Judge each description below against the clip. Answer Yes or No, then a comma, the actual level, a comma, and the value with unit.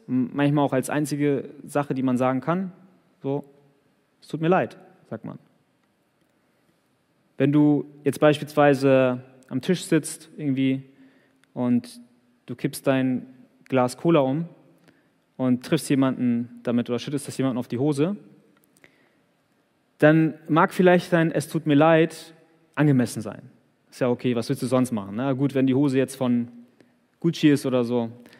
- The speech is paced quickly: No, average, 150 wpm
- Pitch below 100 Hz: No, medium, 140 Hz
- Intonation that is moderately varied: Yes, average, 3.1 semitones